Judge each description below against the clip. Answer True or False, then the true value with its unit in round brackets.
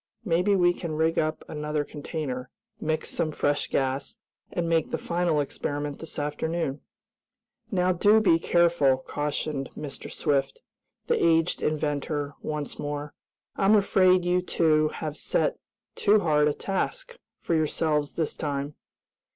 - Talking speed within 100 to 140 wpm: True (135 wpm)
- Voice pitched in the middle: True (155 Hz)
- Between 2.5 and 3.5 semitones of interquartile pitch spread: True (3.0 semitones)